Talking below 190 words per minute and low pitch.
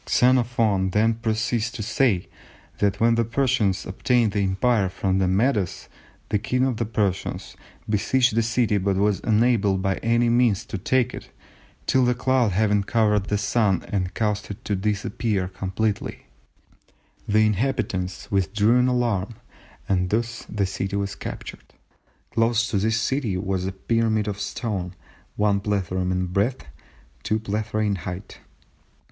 Yes: average, 150 wpm; low, 105 Hz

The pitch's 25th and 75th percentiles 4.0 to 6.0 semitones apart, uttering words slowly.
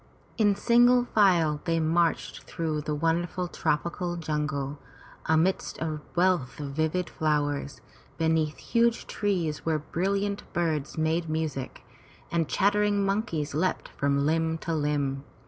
No: average, 3.5 semitones; slow, 125 wpm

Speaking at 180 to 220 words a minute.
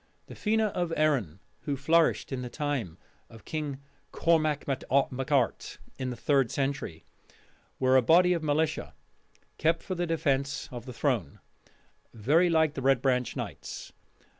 No: average, 150 wpm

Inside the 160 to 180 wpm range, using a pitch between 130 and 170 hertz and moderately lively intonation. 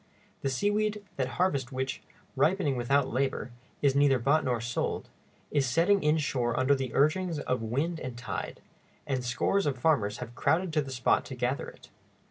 Yes: average, 170 wpm; low, 135 Hz; average, 4.0 semitones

